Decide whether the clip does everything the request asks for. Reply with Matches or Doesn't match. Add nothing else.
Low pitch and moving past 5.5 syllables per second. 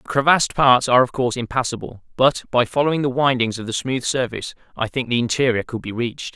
Matches